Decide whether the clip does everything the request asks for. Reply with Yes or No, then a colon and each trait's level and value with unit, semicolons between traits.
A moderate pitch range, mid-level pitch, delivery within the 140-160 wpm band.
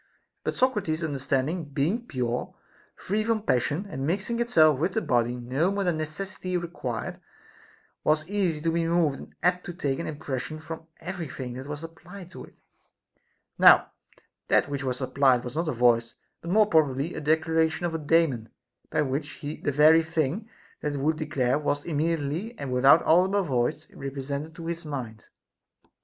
No: average, 3.9 semitones; medium, 155 Hz; average, 170 wpm